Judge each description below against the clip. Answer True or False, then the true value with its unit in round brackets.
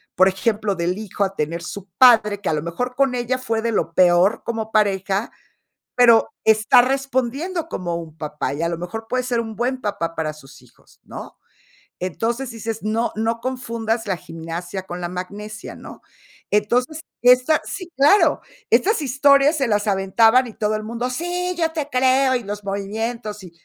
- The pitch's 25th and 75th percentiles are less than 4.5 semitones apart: False (4.8 semitones)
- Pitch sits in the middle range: False (225 Hz)